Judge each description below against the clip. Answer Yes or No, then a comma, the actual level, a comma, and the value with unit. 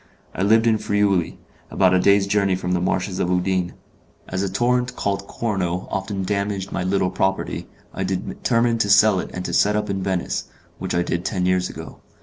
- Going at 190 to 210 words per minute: Yes, average, 195 wpm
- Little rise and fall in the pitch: Yes, narrow, 2.0 semitones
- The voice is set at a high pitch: No, very low, 95 Hz